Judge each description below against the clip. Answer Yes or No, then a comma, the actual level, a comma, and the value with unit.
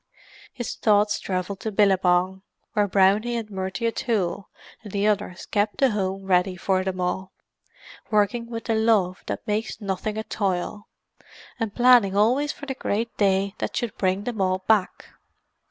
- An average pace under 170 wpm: Yes, average, 160 wpm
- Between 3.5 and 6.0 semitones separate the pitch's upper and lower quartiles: No, average, 2.8 semitones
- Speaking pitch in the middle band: No, high, 205 Hz